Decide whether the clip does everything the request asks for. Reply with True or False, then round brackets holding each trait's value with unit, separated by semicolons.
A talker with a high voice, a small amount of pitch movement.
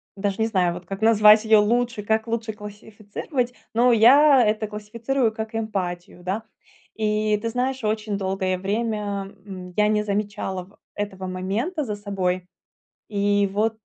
True (210 Hz; 2.1 semitones)